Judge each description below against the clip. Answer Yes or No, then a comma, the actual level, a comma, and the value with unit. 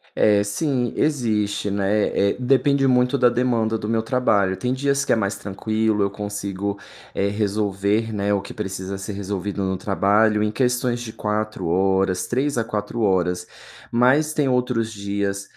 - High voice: No, low, 105 Hz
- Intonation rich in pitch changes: No, average, 3.6 semitones